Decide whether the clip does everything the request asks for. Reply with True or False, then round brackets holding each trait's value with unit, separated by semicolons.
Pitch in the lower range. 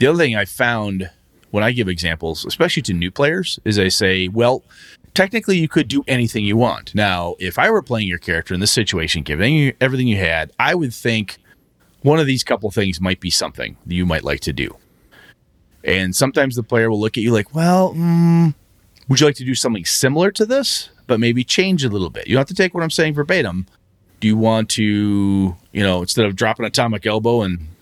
True (110 Hz)